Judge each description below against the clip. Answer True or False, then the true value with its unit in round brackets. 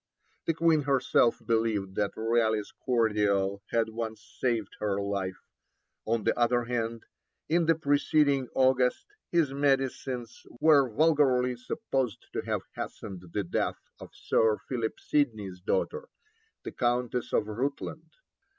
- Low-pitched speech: True (120 Hz)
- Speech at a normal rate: False (125 wpm)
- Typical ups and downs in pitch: True (4.1 semitones)